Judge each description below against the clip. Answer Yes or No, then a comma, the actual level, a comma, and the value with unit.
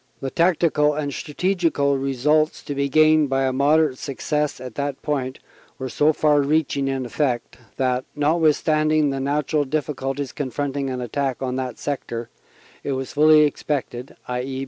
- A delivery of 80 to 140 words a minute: No, average, 150 wpm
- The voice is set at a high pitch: No, medium, 140 Hz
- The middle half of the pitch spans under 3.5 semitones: Yes, narrow, 2.4 semitones